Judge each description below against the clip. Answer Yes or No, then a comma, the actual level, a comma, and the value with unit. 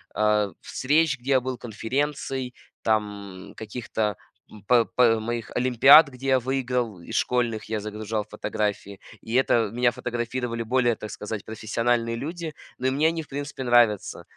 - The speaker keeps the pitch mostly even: No, average, 3.1 semitones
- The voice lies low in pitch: Yes, low, 120 Hz